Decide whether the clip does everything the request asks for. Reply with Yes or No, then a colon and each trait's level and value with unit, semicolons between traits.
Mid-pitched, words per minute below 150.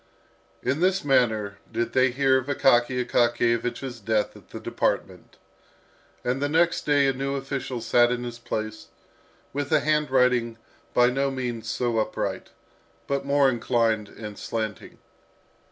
No: low, 125 Hz; average, 140 wpm